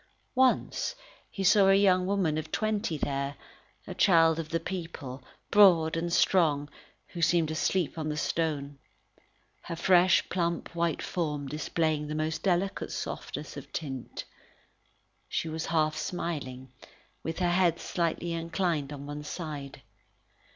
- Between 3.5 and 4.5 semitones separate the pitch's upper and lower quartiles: No, average, 2.7 semitones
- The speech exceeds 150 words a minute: No, slow, 135 wpm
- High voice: No, medium, 165 Hz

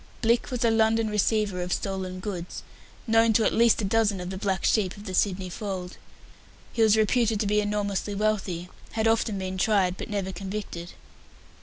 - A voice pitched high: Yes, high, 205 Hz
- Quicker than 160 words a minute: Yes, average, 185 wpm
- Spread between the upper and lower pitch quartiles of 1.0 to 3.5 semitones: Yes, average, 2.8 semitones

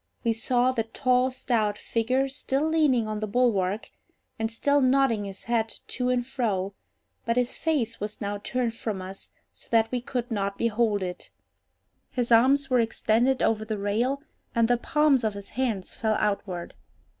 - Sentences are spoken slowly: No, average, 170 wpm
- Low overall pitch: No, high, 230 Hz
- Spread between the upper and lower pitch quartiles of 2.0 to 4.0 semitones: Yes, average, 3.2 semitones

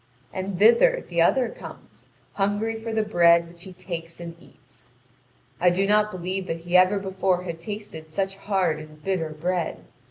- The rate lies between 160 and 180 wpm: Yes, average, 170 wpm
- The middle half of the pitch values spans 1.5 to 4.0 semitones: Yes, average, 3.1 semitones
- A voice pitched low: No, medium, 185 Hz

